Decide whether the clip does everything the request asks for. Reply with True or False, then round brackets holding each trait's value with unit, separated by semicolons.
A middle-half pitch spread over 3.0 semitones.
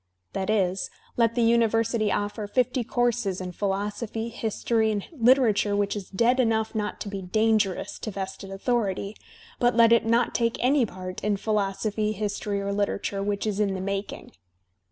False (2.6 semitones)